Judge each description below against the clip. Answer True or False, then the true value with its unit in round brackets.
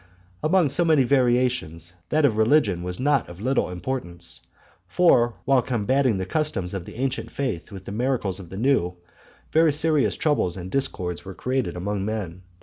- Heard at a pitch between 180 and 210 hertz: False (120 Hz)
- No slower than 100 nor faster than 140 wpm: False (170 wpm)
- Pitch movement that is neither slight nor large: False (6.9 semitones)